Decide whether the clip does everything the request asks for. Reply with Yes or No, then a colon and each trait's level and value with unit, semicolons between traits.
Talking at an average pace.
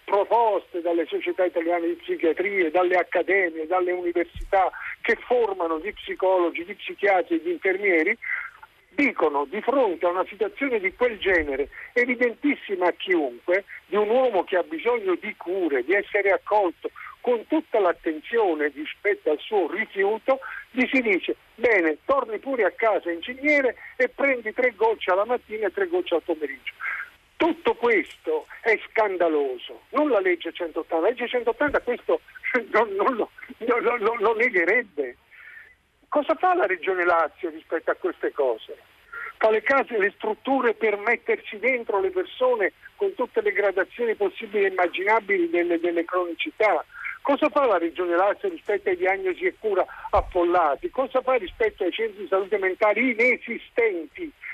Yes: average, 145 wpm